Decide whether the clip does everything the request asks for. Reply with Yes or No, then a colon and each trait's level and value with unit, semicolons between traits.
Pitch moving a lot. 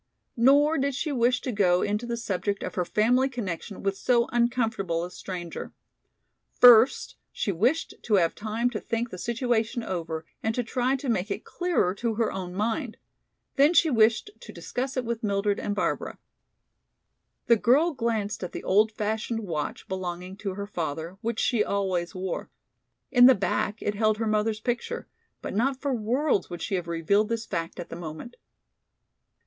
No: average, 4.3 semitones